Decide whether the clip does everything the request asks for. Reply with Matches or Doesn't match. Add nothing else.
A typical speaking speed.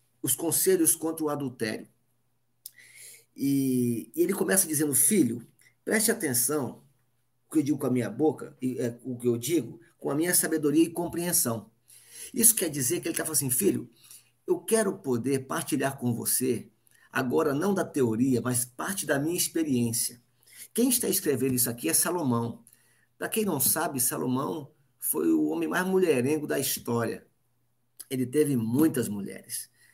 Matches